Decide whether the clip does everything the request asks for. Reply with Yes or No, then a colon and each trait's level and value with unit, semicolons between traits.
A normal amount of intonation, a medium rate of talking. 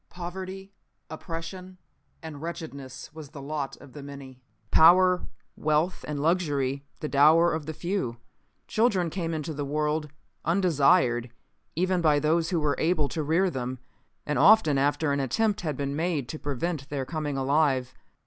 Yes: average, 3.5 semitones; average, 155 wpm